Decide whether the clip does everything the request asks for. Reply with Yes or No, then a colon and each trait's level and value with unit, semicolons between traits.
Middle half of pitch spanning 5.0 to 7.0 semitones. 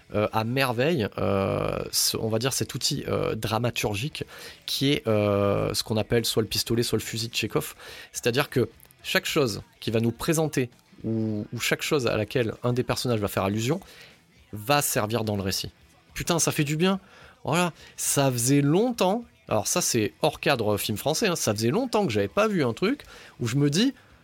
Yes: wide, 5.4 semitones